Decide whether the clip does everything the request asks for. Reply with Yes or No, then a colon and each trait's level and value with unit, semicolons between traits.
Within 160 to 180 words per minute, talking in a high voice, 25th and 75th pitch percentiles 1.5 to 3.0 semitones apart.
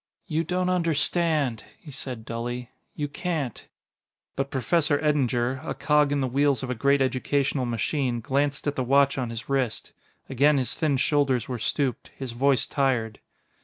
No: average, 165 wpm; low, 135 Hz; average, 2.7 semitones